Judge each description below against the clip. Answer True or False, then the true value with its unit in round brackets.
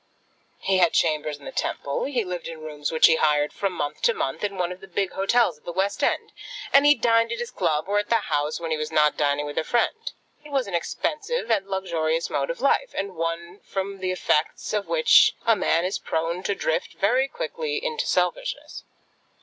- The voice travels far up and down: True (6.5 semitones)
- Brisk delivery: True (220 wpm)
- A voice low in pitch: False (190 Hz)